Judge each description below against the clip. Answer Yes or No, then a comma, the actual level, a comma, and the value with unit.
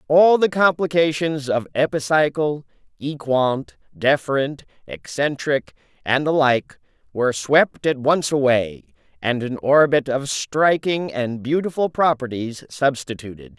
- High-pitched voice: No, medium, 140 Hz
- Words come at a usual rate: No, slow, 110 wpm